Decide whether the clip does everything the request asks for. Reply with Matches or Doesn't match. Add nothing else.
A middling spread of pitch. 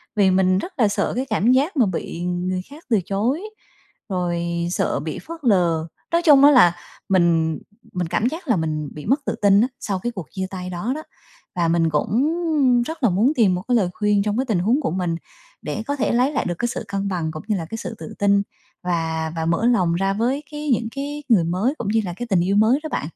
Doesn't match